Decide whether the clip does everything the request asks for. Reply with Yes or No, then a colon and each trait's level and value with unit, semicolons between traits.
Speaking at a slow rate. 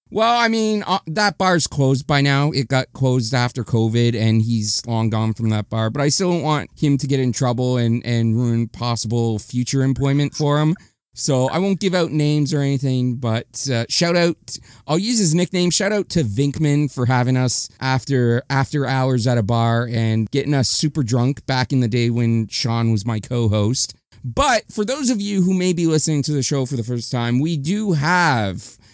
No: fast, 205 wpm